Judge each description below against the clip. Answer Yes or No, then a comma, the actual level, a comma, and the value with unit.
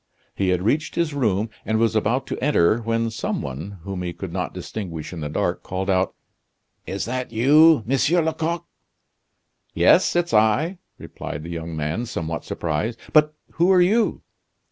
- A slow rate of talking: No, average, 165 wpm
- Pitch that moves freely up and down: Yes, wide, 8.6 semitones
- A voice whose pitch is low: Yes, low, 110 Hz